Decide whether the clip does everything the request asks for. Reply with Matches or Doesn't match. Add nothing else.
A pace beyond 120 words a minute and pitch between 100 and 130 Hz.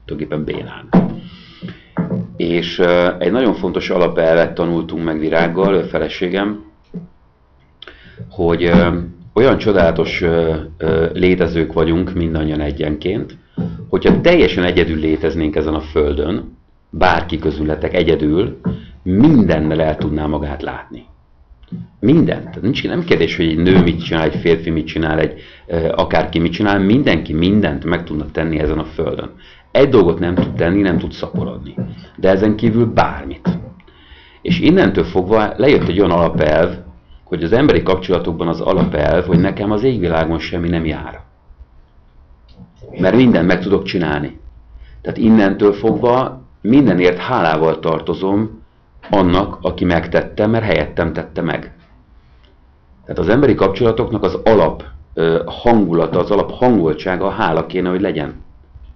Doesn't match